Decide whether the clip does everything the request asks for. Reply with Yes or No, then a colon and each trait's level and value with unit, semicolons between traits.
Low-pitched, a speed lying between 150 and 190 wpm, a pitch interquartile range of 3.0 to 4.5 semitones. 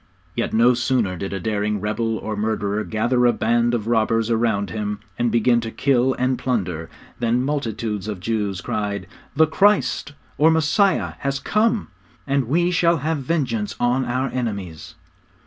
Yes: low, 115 Hz; average, 160 wpm; average, 4.0 semitones